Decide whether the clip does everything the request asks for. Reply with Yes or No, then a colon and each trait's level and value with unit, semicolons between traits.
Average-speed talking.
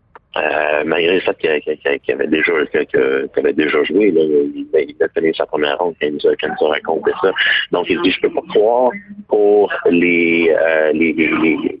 Yes: average, 210 wpm